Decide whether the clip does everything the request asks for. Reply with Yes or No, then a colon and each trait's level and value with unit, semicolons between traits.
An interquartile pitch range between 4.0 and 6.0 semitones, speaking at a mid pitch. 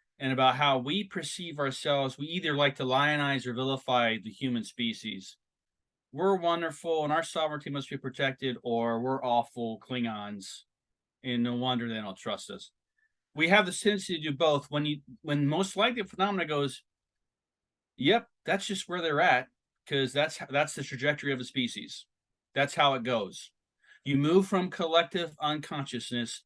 Yes: average, 4.4 semitones; medium, 145 Hz